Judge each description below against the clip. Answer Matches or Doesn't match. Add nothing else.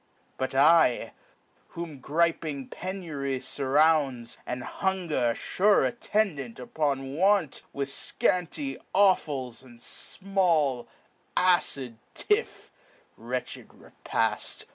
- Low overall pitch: Doesn't match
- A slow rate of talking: Matches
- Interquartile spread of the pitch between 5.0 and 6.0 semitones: Matches